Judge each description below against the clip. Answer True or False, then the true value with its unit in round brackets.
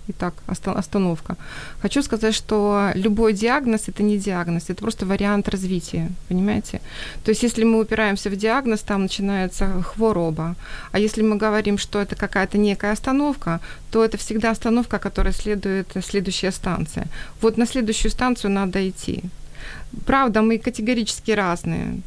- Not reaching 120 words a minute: False (140 wpm)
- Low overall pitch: False (205 Hz)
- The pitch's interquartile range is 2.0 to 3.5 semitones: True (2.5 semitones)